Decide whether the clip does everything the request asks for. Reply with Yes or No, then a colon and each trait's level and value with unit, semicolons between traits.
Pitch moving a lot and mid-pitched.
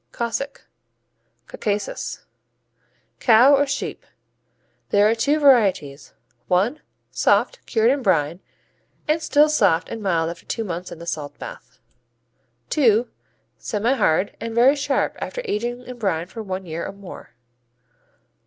No: wide, 6.4 semitones; high, 220 Hz